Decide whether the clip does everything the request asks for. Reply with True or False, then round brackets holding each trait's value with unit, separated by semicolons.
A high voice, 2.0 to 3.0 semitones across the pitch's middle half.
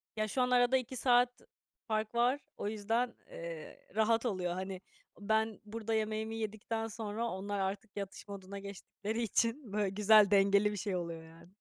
True (215 Hz; 2.4 semitones)